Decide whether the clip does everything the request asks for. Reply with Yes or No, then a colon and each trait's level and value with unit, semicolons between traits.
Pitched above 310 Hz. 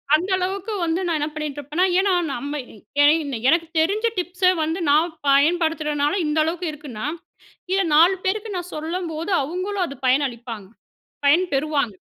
Yes: very high, 320 Hz